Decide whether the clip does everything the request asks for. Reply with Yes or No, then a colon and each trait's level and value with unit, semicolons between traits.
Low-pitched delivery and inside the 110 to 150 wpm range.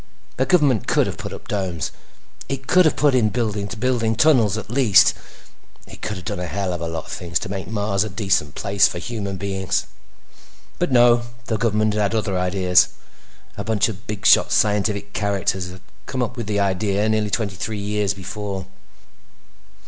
No: low, 105 Hz; average, 185 wpm